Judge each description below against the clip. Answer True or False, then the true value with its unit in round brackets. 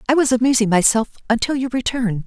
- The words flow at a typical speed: True (185 wpm)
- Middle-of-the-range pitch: False (240 Hz)